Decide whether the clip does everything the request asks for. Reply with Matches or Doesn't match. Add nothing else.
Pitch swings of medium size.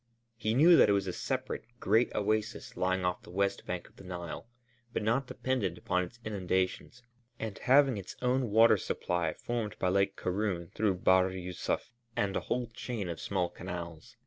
Matches